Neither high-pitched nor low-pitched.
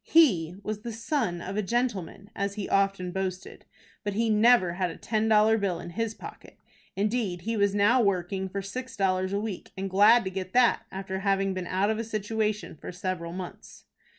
No: high, 200 Hz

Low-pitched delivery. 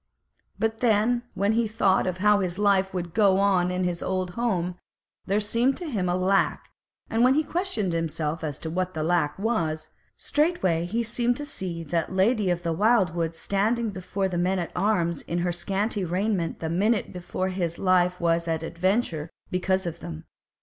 No: medium, 185 Hz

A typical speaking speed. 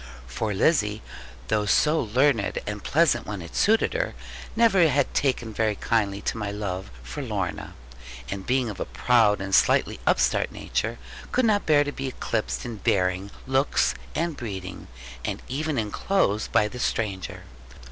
Yes: average, 160 wpm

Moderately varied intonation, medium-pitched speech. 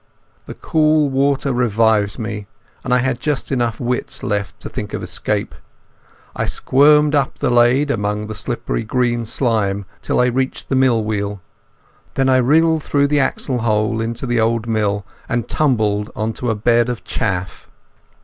No: average, 3.6 semitones; low, 120 Hz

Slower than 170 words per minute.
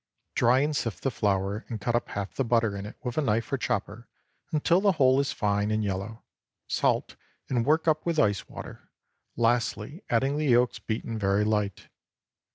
No: average, 185 wpm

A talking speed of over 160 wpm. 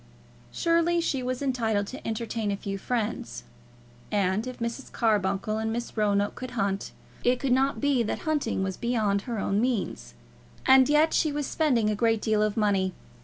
Yes: average, 175 wpm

